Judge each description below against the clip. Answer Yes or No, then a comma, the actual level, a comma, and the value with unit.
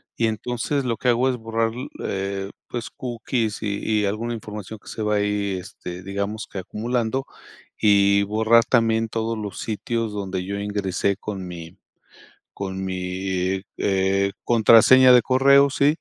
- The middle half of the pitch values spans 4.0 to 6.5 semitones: No, average, 3.0 semitones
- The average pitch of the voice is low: Yes, low, 105 Hz